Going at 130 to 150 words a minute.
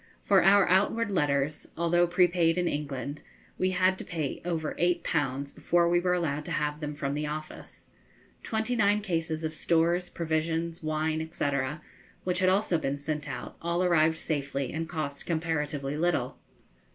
No: average, 165 wpm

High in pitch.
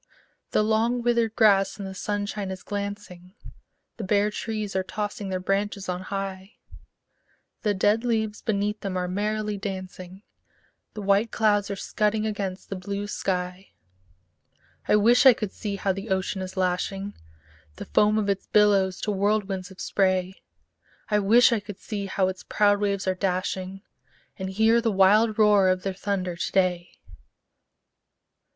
Yes: high, 200 Hz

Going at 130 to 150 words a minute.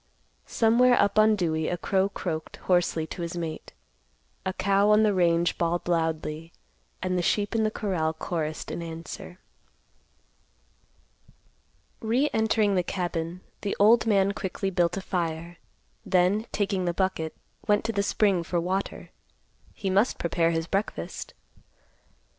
Yes: average, 140 wpm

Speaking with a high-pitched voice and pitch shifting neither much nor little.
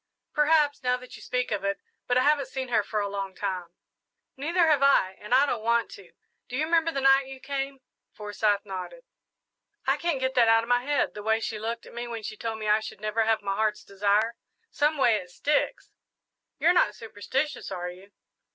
Yes: high, 235 Hz; average, 4.7 semitones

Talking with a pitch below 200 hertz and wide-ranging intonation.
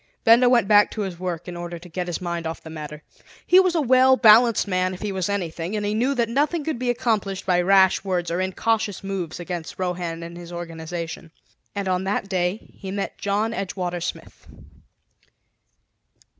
No: high, 190 Hz; average, 3.9 semitones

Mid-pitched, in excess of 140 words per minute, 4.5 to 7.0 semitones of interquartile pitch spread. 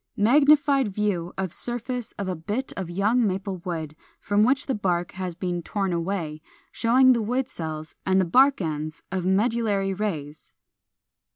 No: high, 195 Hz; average, 160 wpm; average, 5.3 semitones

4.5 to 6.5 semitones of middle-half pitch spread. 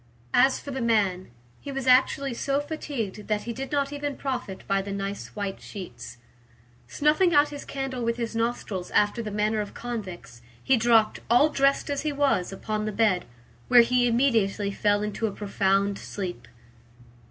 Yes: average, 5.1 semitones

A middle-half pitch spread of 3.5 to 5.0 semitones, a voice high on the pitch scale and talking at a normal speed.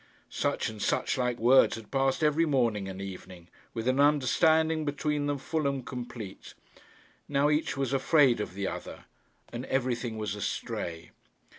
No: average, 4.7 semitones; low, 130 Hz; average, 155 wpm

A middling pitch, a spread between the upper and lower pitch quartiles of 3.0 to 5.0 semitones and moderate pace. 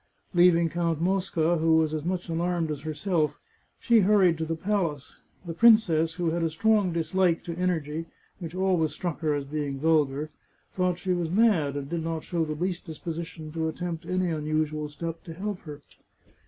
No: medium, 165 Hz; narrow, 2.5 semitones; average, 185 wpm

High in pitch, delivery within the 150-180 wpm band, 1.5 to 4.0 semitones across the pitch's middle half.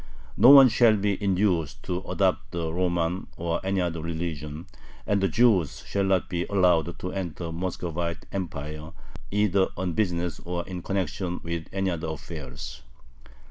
No: very low, 90 Hz; average, 155 wpm; average, 2.7 semitones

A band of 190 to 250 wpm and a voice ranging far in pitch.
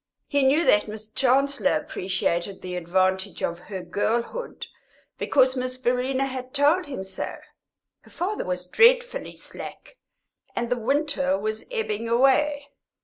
No: slow, 135 wpm; wide, 6.0 semitones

